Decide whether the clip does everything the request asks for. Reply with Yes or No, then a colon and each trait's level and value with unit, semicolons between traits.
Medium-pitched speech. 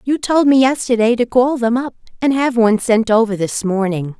No: high, 235 Hz